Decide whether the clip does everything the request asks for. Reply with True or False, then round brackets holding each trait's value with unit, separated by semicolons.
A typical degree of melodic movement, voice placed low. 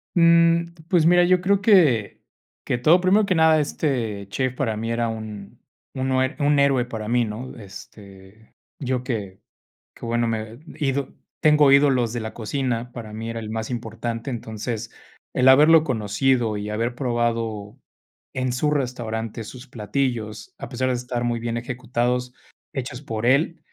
True (3.7 semitones; 120 Hz)